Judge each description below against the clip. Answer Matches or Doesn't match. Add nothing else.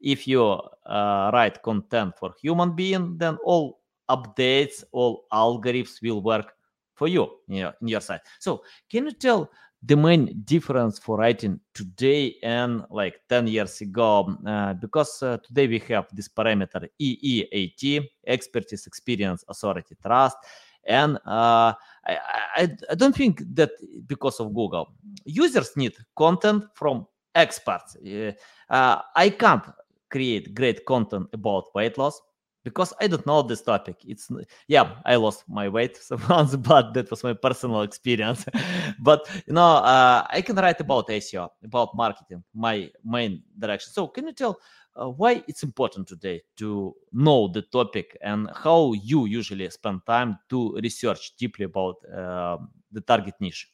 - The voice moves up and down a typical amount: Doesn't match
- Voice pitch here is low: Matches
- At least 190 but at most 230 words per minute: Doesn't match